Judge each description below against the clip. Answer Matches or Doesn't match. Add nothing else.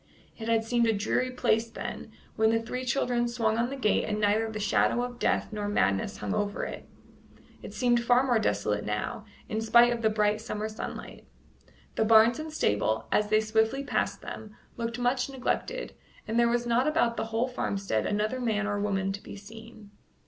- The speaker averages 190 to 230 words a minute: Matches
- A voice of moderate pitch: Doesn't match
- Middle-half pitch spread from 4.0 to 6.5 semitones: Doesn't match